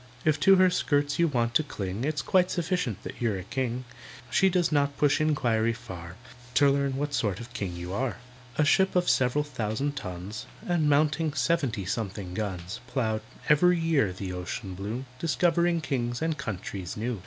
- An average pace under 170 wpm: No, average, 175 wpm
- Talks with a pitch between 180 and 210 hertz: No, low, 130 Hz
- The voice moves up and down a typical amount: No, wide, 6.5 semitones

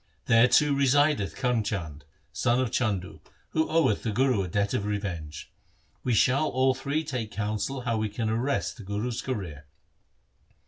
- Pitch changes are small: No, average, 4.3 semitones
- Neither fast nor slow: Yes, average, 165 wpm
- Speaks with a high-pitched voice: No, low, 115 Hz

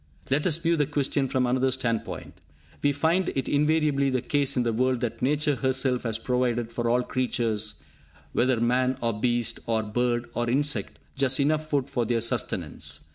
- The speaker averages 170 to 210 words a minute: Yes, average, 180 wpm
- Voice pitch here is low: Yes, low, 130 Hz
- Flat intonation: No, average, 3.1 semitones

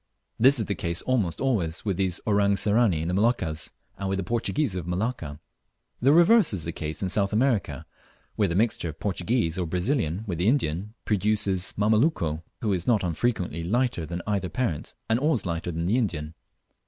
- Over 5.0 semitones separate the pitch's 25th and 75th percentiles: Yes, wide, 5.4 semitones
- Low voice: Yes, low, 100 Hz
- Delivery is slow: No, average, 195 wpm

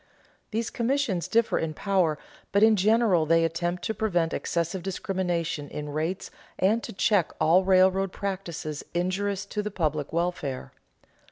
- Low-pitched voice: No, medium, 185 Hz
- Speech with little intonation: No, average, 3.4 semitones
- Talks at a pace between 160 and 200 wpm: No, average, 145 wpm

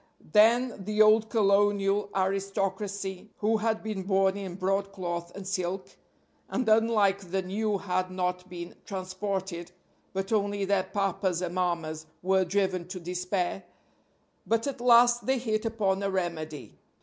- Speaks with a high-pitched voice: Yes, high, 195 Hz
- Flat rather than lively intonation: Yes, narrow, 2.3 semitones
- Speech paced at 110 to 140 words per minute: Yes, slow, 135 wpm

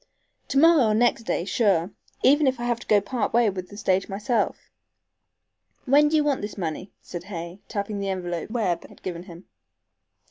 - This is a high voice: Yes, high, 205 Hz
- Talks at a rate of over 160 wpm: Yes, average, 190 wpm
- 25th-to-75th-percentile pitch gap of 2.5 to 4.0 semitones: No, average, 4.7 semitones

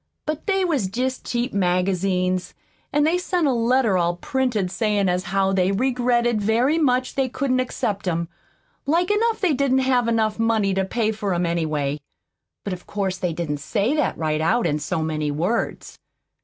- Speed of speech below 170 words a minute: No, average, 185 wpm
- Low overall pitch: No, high, 210 Hz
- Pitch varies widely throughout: Yes, wide, 6.2 semitones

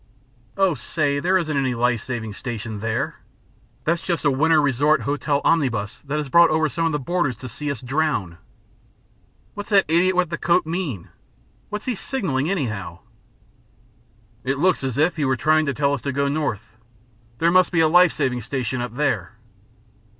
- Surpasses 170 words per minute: Yes, average, 180 wpm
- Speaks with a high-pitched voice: No, medium, 145 Hz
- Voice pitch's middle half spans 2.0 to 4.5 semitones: No, average, 5.0 semitones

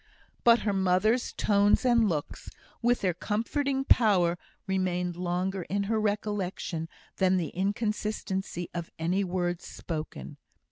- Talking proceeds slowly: Yes, slow, 125 wpm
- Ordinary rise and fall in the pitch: Yes, average, 3.2 semitones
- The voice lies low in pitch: No, high, 190 Hz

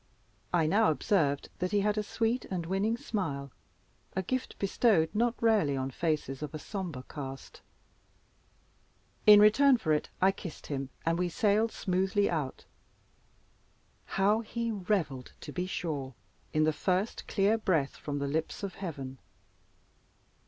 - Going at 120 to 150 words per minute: Yes, average, 145 wpm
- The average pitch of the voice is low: No, medium, 180 Hz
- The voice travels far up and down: Yes, wide, 5.9 semitones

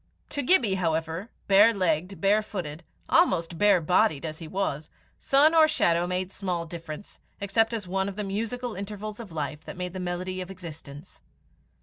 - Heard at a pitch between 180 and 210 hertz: Yes, medium, 185 Hz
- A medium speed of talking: Yes, average, 175 wpm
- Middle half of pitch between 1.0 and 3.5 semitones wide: No, average, 3.9 semitones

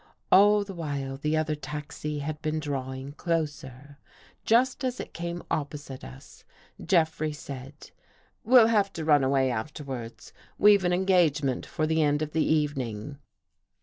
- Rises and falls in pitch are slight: No, average, 3.6 semitones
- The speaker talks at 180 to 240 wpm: No, average, 145 wpm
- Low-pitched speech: No, medium, 150 Hz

